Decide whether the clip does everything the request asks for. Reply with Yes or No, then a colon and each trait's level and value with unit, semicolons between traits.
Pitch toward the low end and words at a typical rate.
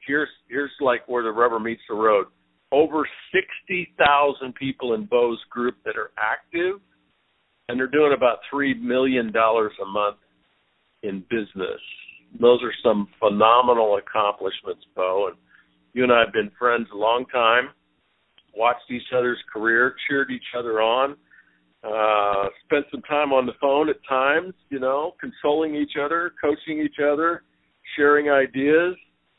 Yes: low, 125 Hz; average, 150 wpm